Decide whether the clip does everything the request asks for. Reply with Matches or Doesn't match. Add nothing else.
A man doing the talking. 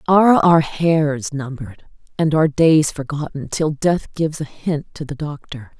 Doesn't match